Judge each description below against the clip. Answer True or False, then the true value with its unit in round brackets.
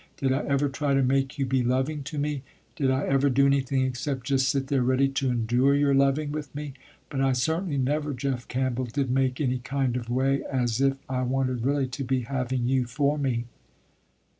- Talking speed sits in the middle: False (210 wpm)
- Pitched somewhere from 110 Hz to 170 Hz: True (135 Hz)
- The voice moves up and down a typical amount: False (1.6 semitones)